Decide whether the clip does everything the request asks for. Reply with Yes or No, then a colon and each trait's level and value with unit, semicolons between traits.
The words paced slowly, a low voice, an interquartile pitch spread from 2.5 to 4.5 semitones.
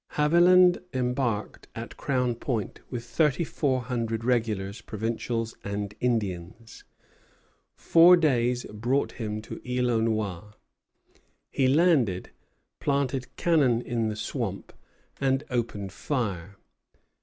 Yes: slow, 110 wpm; low, 120 Hz; average, 3.8 semitones